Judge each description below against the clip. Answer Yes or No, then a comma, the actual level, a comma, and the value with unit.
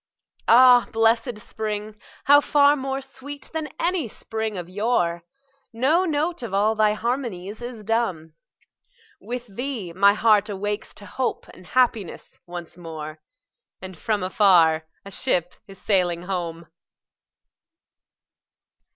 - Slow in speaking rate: Yes, slow, 120 wpm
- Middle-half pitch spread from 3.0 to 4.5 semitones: No, average, 5.2 semitones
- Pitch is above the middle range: Yes, high, 215 Hz